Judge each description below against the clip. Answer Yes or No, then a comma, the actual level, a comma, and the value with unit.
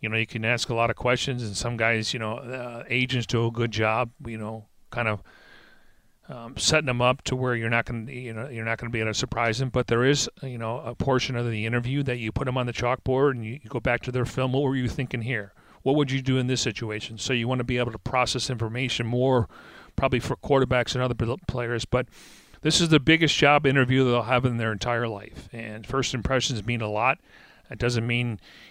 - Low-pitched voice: Yes, low, 120 Hz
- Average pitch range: No, narrow, 2.1 semitones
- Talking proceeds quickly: Yes, fast, 245 wpm